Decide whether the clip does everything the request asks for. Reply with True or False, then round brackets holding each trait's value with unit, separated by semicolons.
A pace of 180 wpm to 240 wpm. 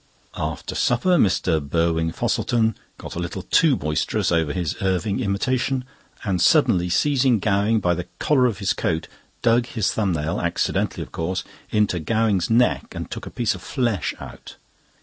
False (165 wpm)